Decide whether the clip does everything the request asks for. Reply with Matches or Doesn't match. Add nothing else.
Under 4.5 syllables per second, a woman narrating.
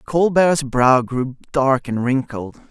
Doesn't match